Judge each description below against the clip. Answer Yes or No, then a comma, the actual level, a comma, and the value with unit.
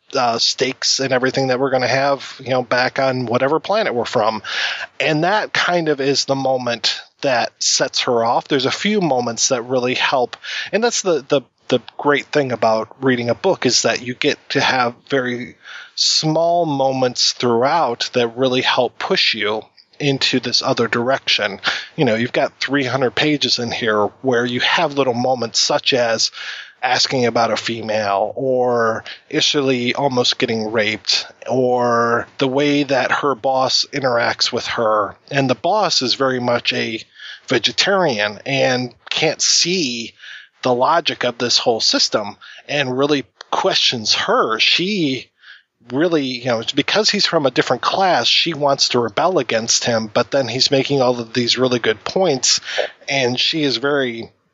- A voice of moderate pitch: No, low, 130 Hz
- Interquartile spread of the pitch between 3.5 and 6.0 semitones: No, average, 2.7 semitones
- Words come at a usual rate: Yes, average, 170 wpm